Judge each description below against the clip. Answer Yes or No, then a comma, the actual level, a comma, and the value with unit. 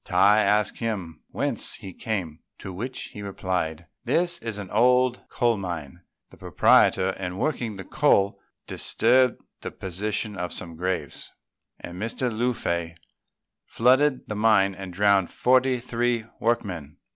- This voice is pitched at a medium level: No, low, 105 Hz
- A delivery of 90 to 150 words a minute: Yes, average, 140 wpm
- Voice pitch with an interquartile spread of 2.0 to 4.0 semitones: No, average, 4.6 semitones